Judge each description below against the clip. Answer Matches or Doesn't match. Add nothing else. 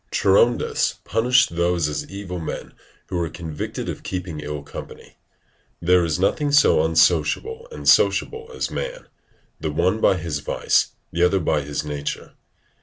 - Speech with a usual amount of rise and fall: Doesn't match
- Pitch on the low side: Matches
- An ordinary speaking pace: Matches